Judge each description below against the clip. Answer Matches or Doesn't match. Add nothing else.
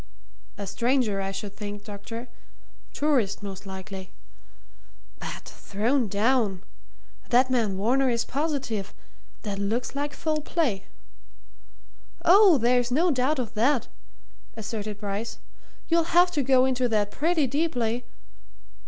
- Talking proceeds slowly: Matches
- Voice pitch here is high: Matches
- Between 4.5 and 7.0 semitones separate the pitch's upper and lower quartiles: Matches